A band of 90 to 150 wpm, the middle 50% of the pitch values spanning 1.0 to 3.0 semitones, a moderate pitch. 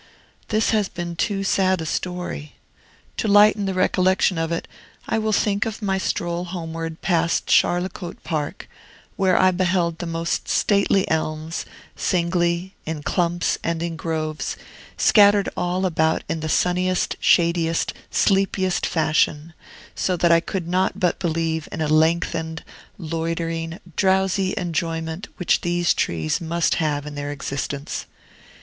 Yes: average, 140 wpm; narrow, 2.5 semitones; medium, 170 Hz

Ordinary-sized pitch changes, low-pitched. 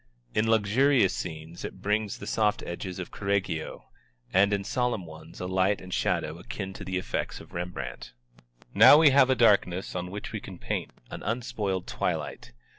Yes: average, 3.4 semitones; low, 100 Hz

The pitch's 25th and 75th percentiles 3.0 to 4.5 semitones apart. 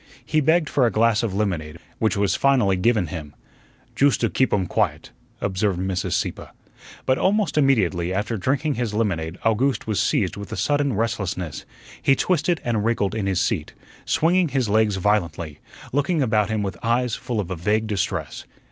No: wide, 5.4 semitones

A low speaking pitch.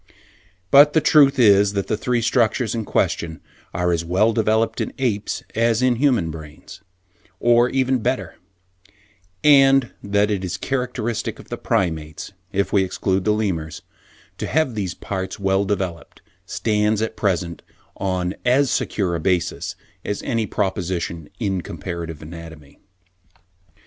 Yes: low, 100 Hz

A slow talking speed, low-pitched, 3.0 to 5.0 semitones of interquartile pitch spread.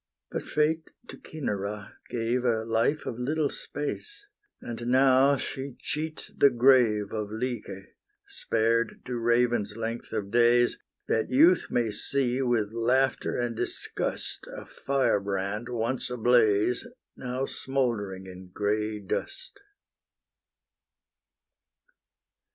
Yes: slow, 110 wpm; low, 120 Hz; average, 3.5 semitones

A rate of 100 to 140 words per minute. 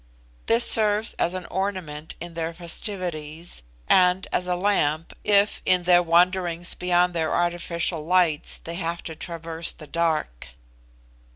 Yes: slow, 135 wpm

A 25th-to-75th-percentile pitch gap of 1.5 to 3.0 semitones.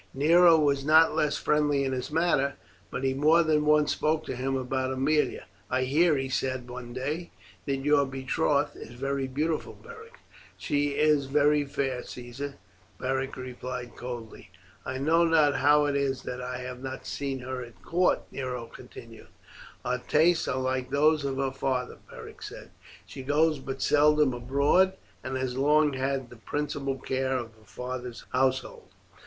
Yes: narrow, 2.5 semitones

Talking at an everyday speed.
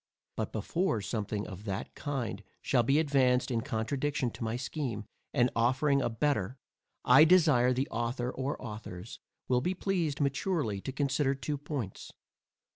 Yes: average, 150 wpm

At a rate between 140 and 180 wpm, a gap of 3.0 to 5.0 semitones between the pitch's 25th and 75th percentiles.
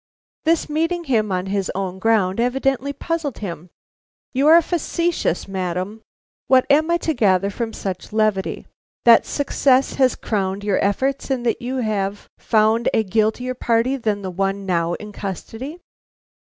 No: average, 155 wpm; wide, 5.5 semitones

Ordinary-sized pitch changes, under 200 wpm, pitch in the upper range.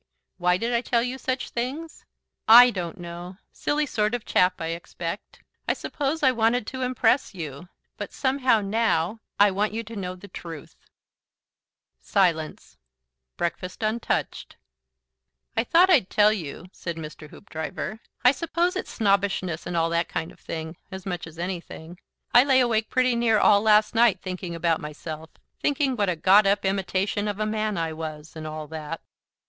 No: wide, 5.7 semitones; average, 170 wpm; high, 200 Hz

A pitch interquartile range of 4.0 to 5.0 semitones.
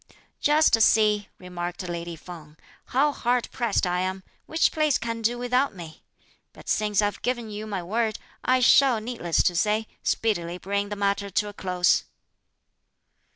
Yes: average, 4.7 semitones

